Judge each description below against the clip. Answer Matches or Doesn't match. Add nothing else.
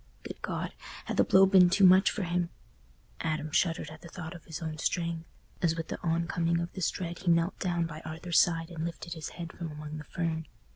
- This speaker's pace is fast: Matches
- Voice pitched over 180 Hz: Doesn't match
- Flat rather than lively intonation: Matches